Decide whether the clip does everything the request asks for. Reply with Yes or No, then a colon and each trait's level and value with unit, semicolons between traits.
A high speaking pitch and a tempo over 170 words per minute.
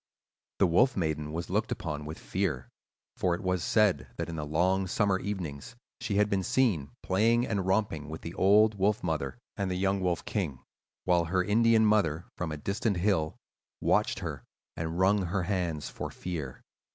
No: very low, 90 Hz; average, 180 wpm